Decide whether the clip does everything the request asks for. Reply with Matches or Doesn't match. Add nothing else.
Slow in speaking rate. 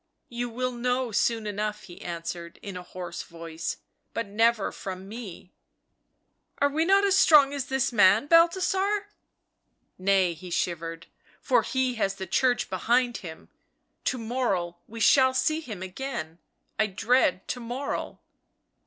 Doesn't match